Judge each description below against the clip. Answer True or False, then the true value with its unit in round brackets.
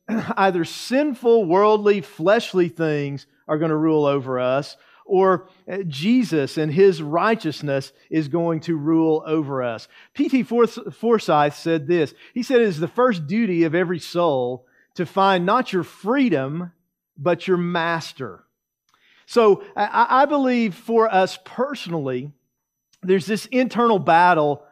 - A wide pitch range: True (6.0 semitones)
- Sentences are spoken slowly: True (130 wpm)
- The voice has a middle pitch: True (180 Hz)